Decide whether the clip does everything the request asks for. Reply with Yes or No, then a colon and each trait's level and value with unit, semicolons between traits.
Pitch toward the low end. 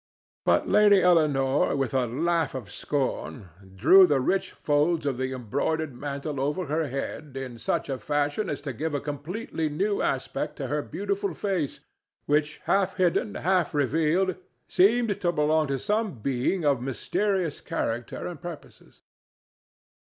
No: medium, 150 Hz